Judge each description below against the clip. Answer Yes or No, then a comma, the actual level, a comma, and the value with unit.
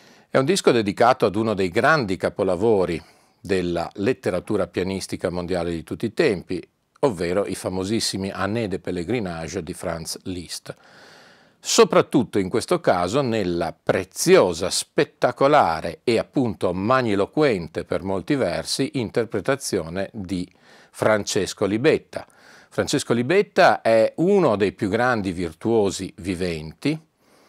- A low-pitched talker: Yes, very low, 95 Hz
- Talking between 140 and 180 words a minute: No, slow, 115 wpm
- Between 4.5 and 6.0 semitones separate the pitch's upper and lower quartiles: No, average, 4.1 semitones